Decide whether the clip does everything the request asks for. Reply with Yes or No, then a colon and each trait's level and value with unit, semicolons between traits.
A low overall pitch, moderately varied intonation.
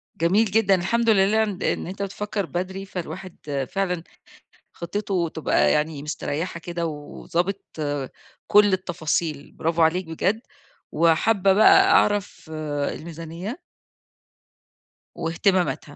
No: medium, 180 Hz; average, 3.3 semitones